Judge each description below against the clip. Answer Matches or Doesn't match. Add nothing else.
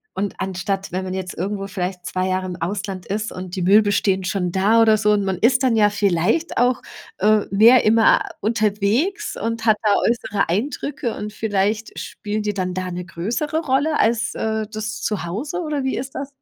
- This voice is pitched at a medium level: Doesn't match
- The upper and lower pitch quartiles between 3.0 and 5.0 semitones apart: Matches